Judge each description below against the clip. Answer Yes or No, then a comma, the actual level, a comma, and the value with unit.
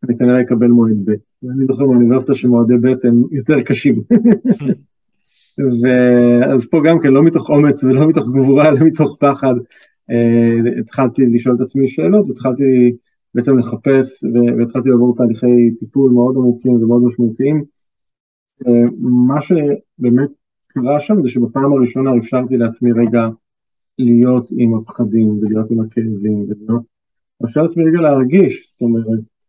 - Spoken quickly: No, average, 135 wpm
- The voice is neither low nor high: No, low, 125 Hz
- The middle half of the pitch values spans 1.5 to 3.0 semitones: Yes, narrow, 2.5 semitones